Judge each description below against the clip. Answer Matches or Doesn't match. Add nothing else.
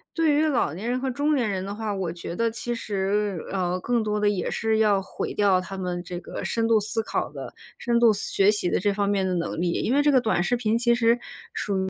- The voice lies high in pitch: Matches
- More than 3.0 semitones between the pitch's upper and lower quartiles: Matches